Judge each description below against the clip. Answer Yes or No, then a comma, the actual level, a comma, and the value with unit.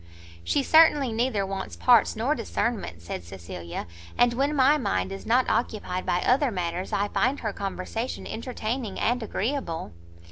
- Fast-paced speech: No, average, 150 wpm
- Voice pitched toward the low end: No, high, 225 Hz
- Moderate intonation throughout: No, wide, 5.8 semitones